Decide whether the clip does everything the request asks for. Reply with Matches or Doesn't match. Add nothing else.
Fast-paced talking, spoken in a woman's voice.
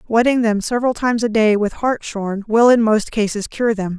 Matches